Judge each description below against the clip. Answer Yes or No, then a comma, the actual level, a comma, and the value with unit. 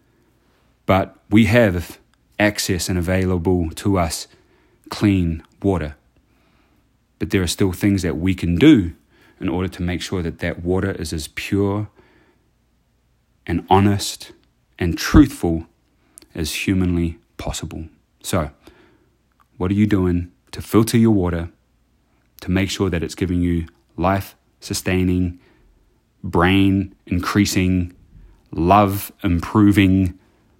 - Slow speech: Yes, slow, 115 wpm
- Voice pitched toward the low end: Yes, very low, 95 Hz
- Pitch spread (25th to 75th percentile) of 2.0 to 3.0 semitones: Yes, narrow, 2.5 semitones